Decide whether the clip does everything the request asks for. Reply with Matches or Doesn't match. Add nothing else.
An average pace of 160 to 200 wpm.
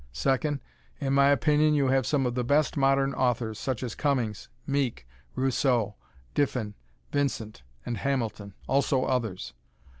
Doesn't match